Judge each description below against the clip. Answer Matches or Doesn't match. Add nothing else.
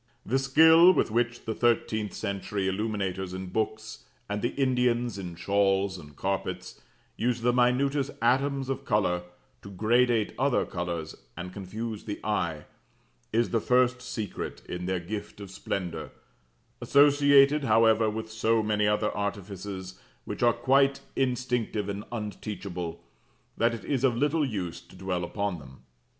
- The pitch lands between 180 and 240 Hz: Doesn't match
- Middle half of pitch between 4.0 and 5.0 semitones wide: Matches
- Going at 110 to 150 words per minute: Matches